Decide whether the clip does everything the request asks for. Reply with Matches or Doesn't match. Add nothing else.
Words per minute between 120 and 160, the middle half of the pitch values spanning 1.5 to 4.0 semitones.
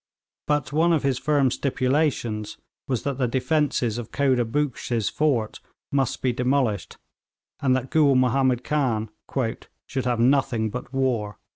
Matches